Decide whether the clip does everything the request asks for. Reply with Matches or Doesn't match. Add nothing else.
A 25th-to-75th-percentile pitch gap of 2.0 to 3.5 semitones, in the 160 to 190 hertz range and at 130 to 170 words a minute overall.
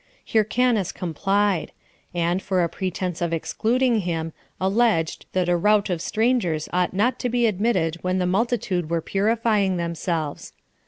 Doesn't match